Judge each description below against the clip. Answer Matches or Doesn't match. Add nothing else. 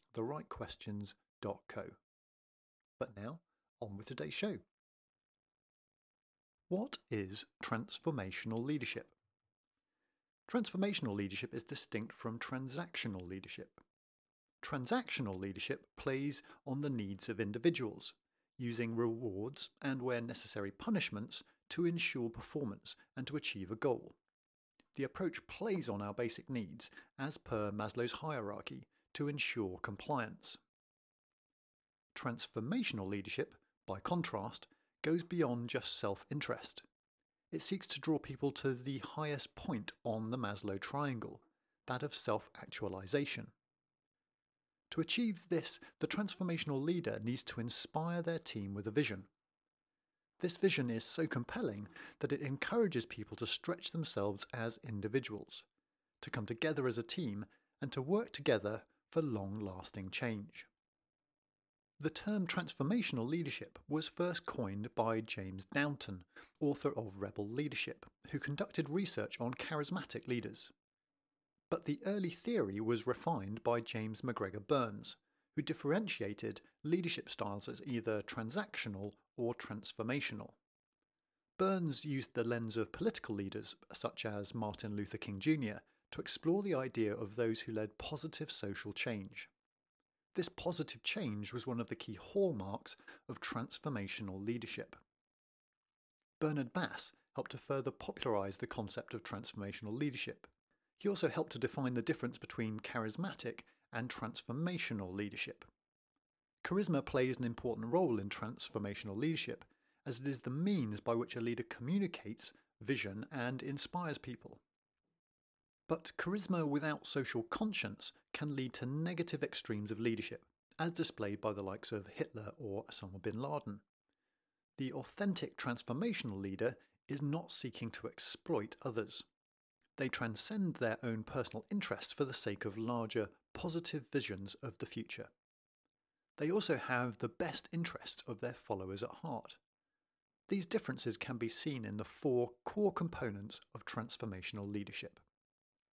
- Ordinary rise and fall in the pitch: Doesn't match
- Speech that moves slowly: Matches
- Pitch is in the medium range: Doesn't match